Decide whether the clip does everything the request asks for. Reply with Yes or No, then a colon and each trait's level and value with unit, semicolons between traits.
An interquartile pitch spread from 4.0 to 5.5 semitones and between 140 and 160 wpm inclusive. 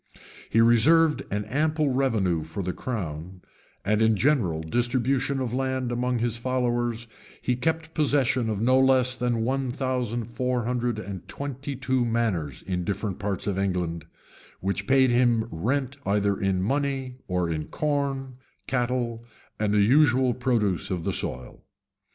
Yes: average, 4.5 semitones; average, 150 wpm